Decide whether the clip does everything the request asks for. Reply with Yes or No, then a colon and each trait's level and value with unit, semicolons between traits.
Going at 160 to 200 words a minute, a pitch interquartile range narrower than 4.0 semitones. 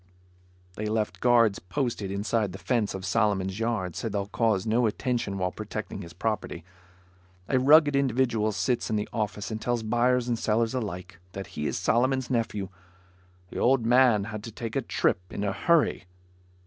Yes: average, 175 wpm; average, 3.3 semitones